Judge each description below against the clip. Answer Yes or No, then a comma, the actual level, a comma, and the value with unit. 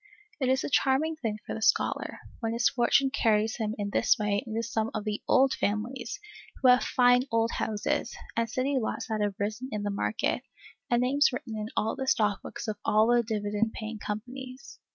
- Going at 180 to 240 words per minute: Yes, average, 200 wpm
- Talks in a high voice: Yes, high, 225 Hz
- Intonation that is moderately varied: Yes, average, 3.1 semitones